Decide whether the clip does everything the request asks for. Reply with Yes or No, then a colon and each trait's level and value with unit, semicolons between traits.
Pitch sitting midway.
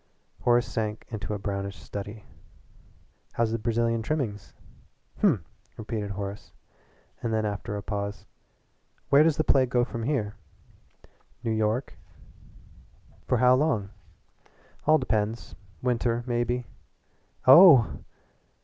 No: low, 115 Hz